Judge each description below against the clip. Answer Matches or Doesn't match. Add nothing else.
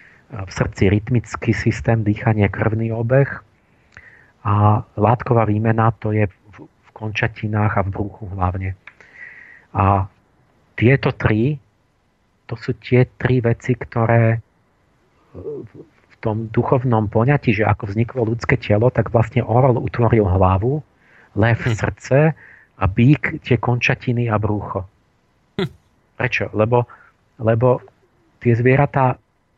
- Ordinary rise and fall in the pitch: Matches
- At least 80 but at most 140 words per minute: Matches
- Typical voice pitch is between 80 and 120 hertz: Matches